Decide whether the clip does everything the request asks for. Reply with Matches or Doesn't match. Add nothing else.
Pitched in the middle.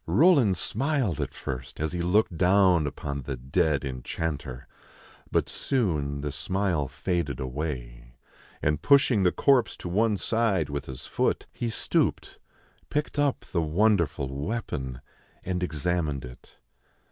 Doesn't match